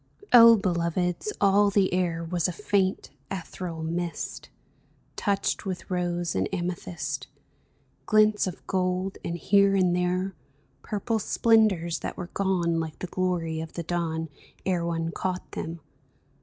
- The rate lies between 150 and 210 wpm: No, average, 140 wpm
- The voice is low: No, medium, 180 Hz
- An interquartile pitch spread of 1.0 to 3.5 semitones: Yes, narrow, 2.4 semitones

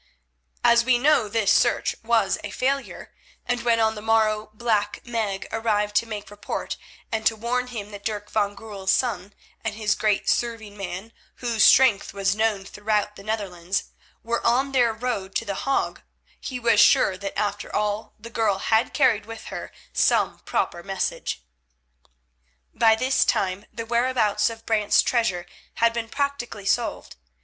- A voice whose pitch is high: Yes, high, 220 Hz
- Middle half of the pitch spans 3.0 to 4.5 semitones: No, narrow, 2.4 semitones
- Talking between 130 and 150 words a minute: No, average, 165 wpm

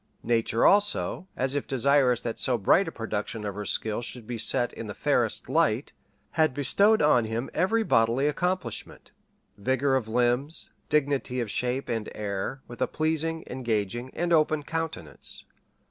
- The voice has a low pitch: Yes, low, 130 Hz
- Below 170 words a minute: Yes, average, 160 wpm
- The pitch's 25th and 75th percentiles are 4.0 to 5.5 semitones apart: Yes, average, 5.0 semitones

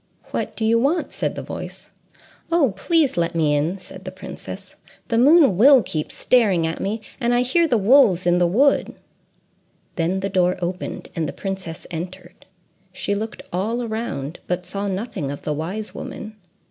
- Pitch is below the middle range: No, high, 195 Hz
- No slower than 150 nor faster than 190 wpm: Yes, average, 175 wpm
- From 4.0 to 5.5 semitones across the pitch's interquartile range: Yes, average, 5.2 semitones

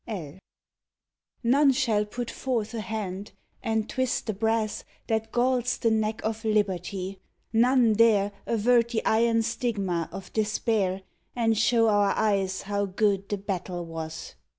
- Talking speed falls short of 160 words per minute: Yes, average, 140 wpm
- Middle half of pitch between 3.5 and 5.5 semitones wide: No, average, 2.7 semitones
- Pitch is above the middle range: Yes, high, 215 Hz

